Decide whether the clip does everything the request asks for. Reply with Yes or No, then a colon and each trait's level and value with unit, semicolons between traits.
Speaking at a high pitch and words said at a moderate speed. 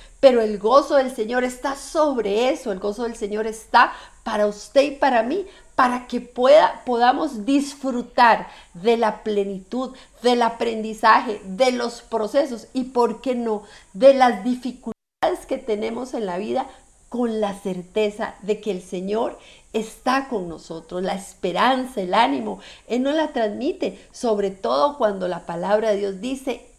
Yes: high, 235 Hz; average, 155 wpm